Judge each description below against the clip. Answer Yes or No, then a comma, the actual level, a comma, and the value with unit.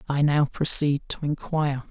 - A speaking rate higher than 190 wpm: No, average, 155 wpm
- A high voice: No, medium, 145 Hz